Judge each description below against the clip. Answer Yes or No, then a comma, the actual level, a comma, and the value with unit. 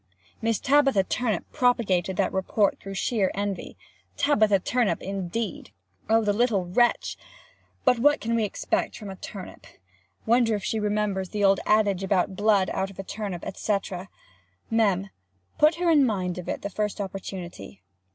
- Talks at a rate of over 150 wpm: Yes, average, 160 wpm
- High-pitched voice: Yes, high, 205 Hz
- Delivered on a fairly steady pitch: No, average, 3.0 semitones